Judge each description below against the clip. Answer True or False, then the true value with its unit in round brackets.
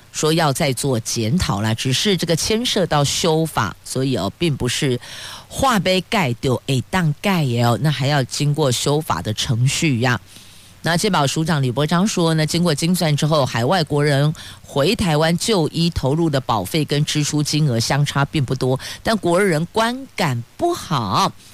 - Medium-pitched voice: True (150 Hz)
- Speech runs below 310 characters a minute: True (250 characters per minute)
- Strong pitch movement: False (4.7 semitones)